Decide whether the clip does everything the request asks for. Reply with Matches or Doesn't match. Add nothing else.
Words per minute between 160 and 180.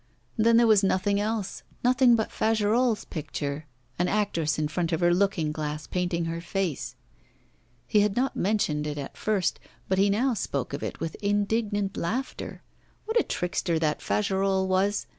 Matches